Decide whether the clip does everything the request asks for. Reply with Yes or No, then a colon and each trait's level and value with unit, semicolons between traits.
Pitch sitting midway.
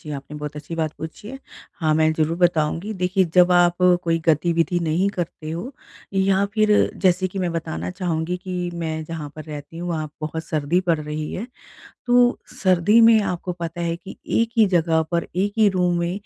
Yes: medium, 170 Hz